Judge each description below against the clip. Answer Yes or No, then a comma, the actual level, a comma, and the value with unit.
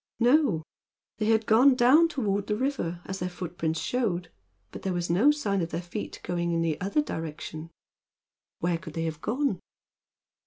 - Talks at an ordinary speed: Yes, average, 170 wpm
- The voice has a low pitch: No, high, 190 Hz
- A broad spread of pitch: Yes, wide, 6.3 semitones